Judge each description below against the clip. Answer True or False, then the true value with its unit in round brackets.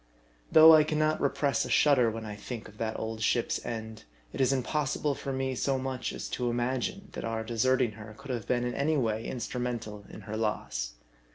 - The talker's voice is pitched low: True (120 Hz)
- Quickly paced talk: True (210 wpm)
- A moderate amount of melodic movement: True (3.6 semitones)